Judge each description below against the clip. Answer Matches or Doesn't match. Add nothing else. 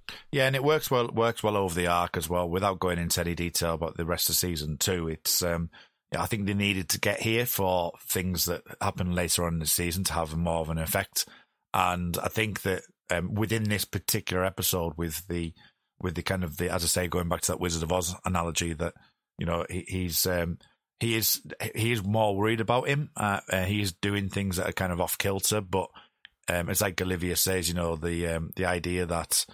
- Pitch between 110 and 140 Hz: Doesn't match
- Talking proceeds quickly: Matches